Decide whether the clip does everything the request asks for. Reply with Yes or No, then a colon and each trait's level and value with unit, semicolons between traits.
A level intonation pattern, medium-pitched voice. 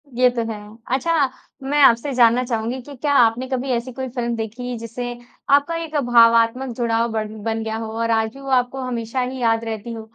No: narrow, 2.2 semitones; high, 240 Hz